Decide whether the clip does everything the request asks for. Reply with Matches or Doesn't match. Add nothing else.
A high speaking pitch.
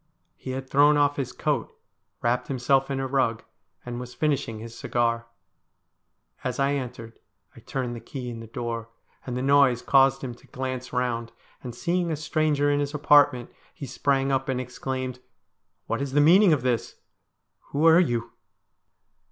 Doesn't match